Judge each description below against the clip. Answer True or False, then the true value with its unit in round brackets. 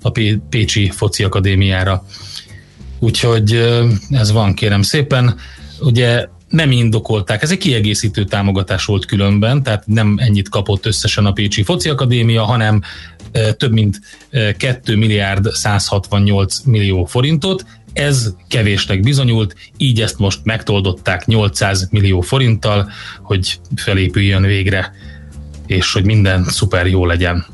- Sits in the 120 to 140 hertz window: False (105 Hz)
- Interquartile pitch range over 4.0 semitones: False (2.8 semitones)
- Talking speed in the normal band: True (120 wpm)